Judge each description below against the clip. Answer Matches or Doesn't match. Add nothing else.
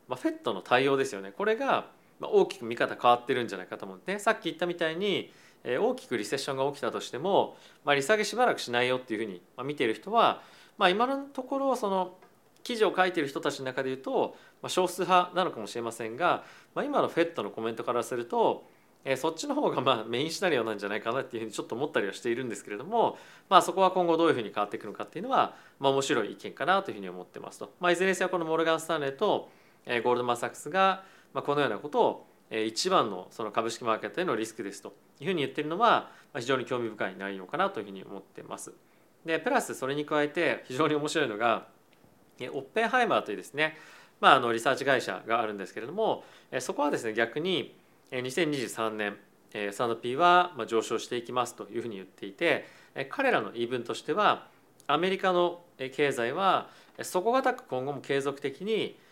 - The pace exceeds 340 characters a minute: Matches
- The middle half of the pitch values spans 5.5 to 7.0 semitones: Doesn't match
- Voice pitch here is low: Doesn't match